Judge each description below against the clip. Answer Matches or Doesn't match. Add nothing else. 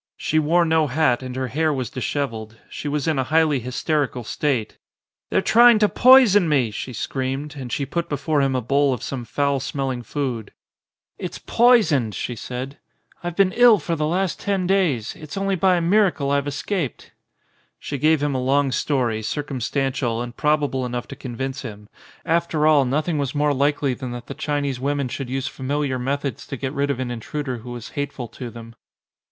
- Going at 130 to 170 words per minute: Doesn't match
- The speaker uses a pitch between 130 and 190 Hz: Matches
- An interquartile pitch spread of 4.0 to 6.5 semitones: Doesn't match